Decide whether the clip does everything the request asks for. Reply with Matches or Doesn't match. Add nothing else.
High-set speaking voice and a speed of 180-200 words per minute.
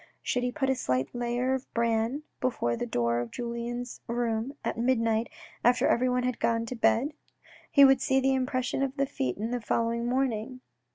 Matches